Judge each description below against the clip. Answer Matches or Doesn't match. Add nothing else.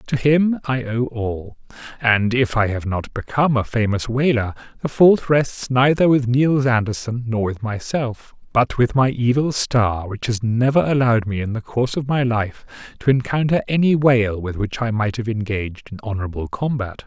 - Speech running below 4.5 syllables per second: Doesn't match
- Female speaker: Doesn't match